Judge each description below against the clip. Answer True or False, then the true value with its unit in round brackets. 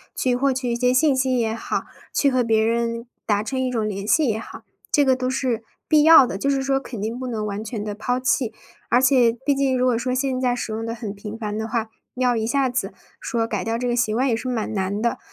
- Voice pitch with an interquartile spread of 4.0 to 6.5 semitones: False (2.7 semitones)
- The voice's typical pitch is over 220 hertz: True (240 Hz)